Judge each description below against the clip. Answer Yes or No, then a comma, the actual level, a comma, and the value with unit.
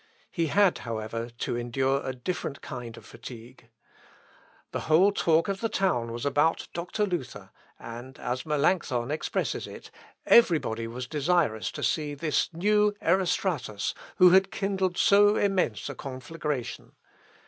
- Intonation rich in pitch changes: Yes, wide, 7.2 semitones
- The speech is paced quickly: No, average, 140 wpm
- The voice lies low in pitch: No, medium, 150 Hz